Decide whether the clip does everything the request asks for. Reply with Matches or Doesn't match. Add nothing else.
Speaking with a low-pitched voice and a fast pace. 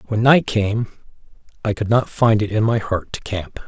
Matches